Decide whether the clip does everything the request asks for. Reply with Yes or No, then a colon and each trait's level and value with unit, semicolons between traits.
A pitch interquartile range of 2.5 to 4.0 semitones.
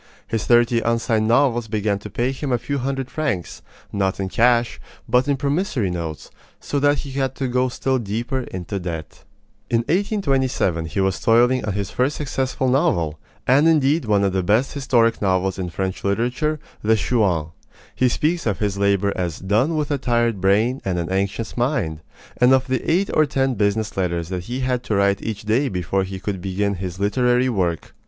No: average, 5.2 semitones